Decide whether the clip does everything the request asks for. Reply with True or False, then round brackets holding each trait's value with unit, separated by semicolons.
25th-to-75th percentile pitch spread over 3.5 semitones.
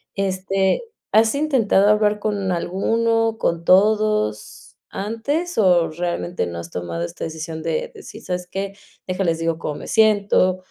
True (4.3 semitones)